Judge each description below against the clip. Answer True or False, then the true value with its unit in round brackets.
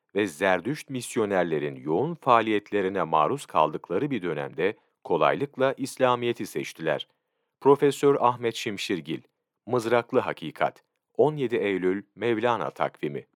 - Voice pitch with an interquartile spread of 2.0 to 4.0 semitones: True (3.5 semitones)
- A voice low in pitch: True (120 Hz)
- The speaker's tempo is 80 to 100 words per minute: True (95 wpm)